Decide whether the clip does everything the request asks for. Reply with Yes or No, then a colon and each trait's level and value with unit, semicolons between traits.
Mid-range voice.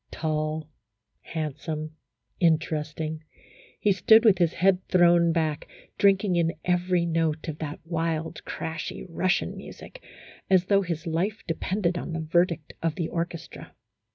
Yes: medium, 165 Hz